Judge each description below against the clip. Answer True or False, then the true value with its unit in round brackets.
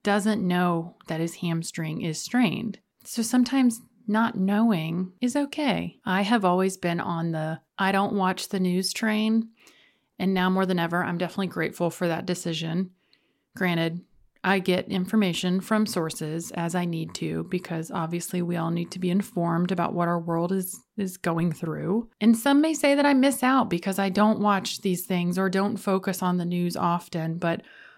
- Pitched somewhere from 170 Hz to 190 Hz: True (185 Hz)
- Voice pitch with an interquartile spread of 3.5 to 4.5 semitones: True (3.9 semitones)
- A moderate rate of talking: True (180 wpm)